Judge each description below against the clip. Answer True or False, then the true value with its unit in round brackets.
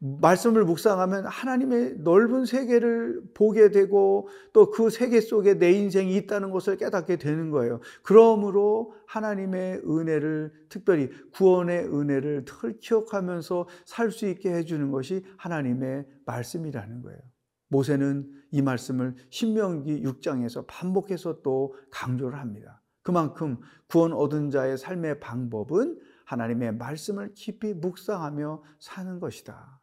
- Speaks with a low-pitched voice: False (170 Hz)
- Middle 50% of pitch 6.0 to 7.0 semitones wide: True (6.6 semitones)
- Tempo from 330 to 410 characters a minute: False (295 characters per minute)